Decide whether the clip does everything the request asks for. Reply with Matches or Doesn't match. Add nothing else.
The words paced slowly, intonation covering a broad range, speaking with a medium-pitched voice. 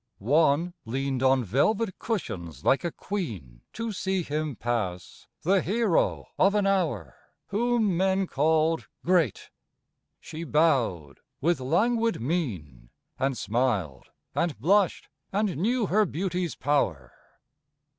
Matches